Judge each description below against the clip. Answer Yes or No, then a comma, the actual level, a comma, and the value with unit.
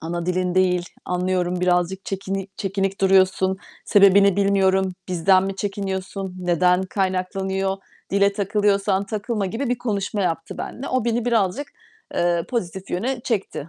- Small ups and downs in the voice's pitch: Yes, narrow, 1.6 semitones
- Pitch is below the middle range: No, high, 190 Hz